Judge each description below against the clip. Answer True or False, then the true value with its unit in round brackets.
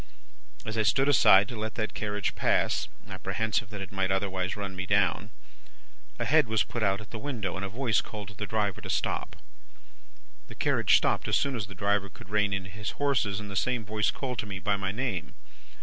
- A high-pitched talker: False (105 Hz)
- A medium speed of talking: False (215 wpm)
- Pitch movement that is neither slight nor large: False (2.2 semitones)